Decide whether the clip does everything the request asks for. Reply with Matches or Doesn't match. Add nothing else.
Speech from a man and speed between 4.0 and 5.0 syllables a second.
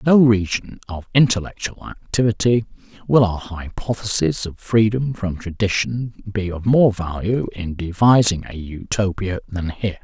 Matches